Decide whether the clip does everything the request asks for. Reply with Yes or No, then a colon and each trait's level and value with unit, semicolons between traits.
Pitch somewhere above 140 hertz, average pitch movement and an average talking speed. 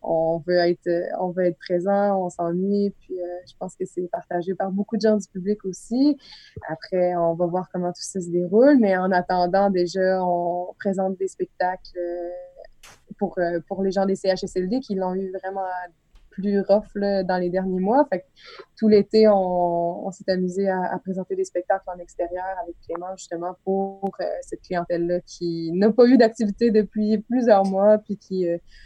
No: high, 190 Hz; narrow, 2.2 semitones; average, 195 wpm